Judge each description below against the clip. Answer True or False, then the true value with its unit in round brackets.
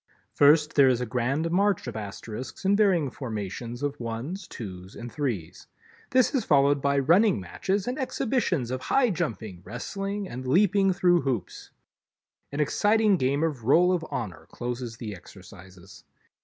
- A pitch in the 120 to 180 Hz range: True (140 Hz)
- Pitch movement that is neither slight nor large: False (8.1 semitones)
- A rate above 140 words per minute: True (155 wpm)